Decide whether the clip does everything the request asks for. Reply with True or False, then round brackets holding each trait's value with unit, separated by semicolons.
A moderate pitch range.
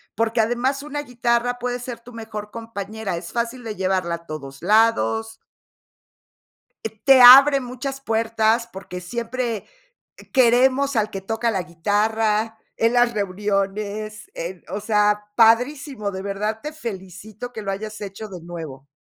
True (3.3 semitones)